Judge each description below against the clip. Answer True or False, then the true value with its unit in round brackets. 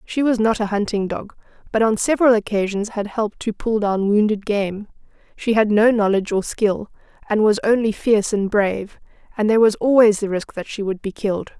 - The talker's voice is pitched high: True (210 Hz)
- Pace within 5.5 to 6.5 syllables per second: True (5.6 syllables/s)